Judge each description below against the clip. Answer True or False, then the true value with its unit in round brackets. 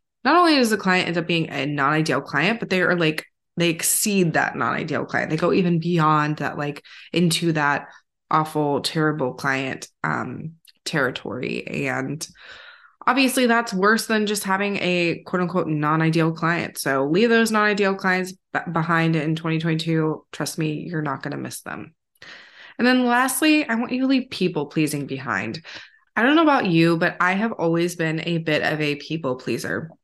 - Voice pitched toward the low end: False (165 Hz)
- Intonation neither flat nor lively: True (4.5 semitones)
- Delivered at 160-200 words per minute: True (180 wpm)